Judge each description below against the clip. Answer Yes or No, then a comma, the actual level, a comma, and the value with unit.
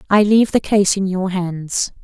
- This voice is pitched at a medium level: No, high, 195 Hz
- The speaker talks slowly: No, fast, 205 wpm